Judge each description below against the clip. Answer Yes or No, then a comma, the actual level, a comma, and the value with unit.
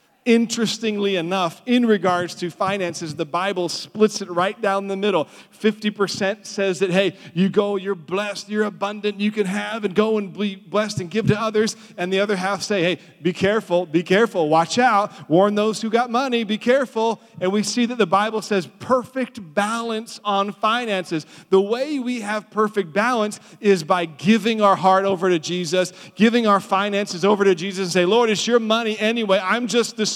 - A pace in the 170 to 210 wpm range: Yes, average, 190 wpm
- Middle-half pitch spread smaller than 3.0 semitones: Yes, narrow, 2.5 semitones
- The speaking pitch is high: Yes, high, 205 Hz